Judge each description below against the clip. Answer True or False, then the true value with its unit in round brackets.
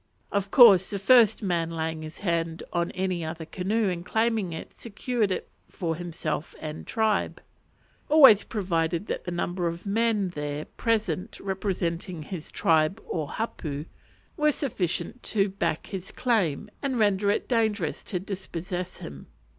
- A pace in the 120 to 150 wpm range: True (145 wpm)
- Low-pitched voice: False (185 Hz)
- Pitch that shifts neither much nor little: True (4.3 semitones)